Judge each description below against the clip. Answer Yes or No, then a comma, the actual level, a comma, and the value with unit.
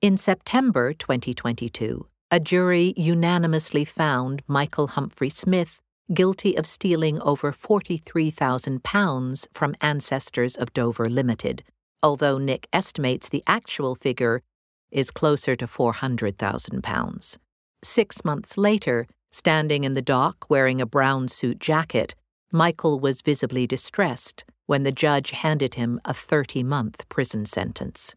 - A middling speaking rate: No, slow, 115 wpm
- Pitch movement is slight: No, average, 4.4 semitones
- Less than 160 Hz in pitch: Yes, medium, 140 Hz